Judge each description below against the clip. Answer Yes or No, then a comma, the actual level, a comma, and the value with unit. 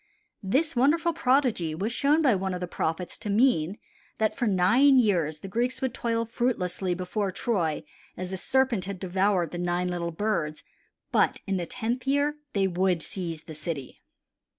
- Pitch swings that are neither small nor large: No, wide, 5.7 semitones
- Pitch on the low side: No, high, 195 Hz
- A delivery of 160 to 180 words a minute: Yes, average, 175 wpm